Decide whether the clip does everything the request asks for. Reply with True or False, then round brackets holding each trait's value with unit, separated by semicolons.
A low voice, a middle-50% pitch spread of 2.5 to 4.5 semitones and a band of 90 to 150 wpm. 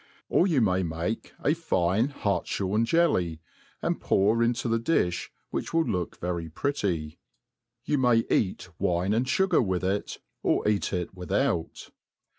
False (100 Hz; 5.5 semitones; 145 wpm)